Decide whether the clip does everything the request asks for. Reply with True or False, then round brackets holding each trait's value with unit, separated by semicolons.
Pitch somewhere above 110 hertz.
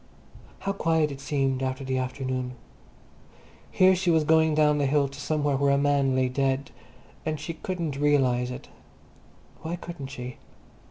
True (140 Hz)